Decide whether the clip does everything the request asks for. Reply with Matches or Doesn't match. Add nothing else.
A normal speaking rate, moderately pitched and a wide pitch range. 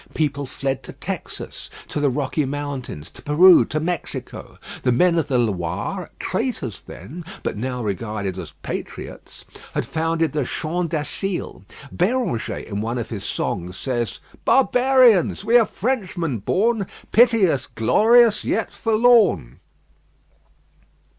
Doesn't match